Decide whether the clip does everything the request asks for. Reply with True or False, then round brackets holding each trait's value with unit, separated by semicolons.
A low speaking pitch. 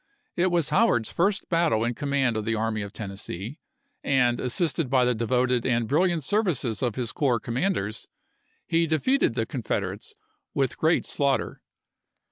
True (130 Hz)